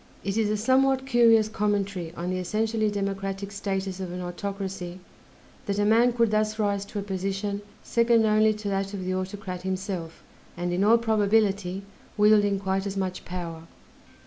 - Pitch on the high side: Yes, high, 200 Hz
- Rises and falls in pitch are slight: Yes, narrow, 2.1 semitones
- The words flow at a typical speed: Yes, average, 170 wpm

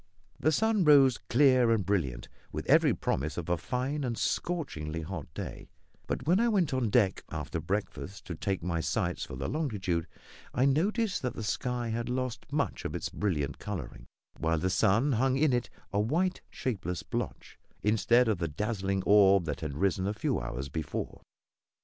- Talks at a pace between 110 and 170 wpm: No, average, 180 wpm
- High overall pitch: No, low, 105 Hz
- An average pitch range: No, wide, 7.5 semitones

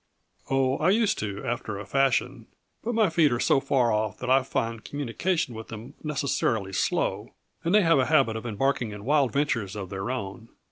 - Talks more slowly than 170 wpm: No, average, 195 wpm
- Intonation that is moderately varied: Yes, average, 4.8 semitones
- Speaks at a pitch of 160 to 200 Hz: No, low, 125 Hz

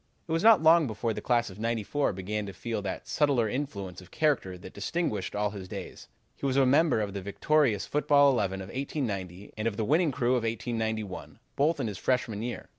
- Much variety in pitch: Yes, wide, 5.7 semitones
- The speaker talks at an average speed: No, fast, 210 wpm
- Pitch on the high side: No, low, 115 Hz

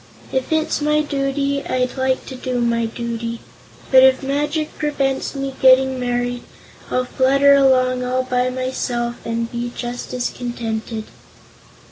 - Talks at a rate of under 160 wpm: Yes, average, 140 wpm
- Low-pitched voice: No, very high, 255 Hz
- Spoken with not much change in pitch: Yes, narrow, 2.1 semitones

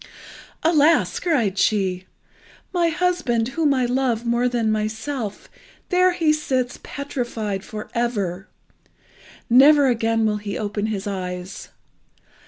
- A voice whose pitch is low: No, high, 235 Hz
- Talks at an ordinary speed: No, slow, 115 wpm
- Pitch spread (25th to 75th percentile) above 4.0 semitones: Yes, average, 5.3 semitones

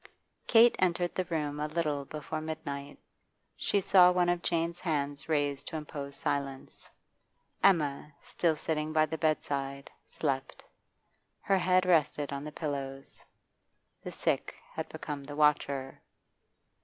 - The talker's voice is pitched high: No, medium, 150 Hz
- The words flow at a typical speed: No, slow, 130 wpm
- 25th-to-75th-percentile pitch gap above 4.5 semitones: No, average, 3.1 semitones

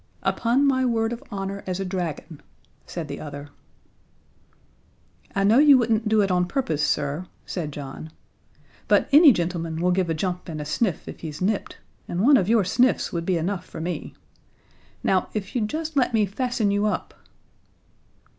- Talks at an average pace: Yes, average, 175 wpm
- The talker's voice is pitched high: Yes, high, 195 Hz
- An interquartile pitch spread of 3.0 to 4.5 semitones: No, wide, 5.4 semitones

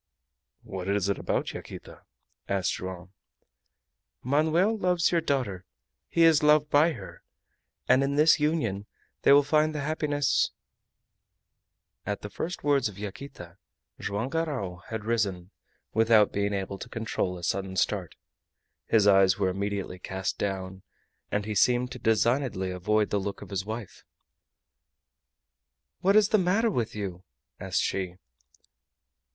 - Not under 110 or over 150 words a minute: Yes, average, 140 wpm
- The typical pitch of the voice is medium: No, low, 105 Hz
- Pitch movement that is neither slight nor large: No, wide, 7.1 semitones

